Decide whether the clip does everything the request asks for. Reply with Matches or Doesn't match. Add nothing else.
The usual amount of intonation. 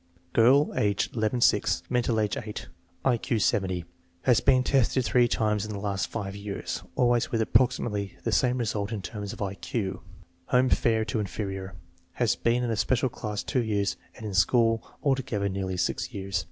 Matches